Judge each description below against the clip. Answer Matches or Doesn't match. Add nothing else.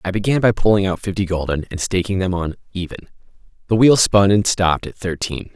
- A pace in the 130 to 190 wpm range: Doesn't match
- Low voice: Matches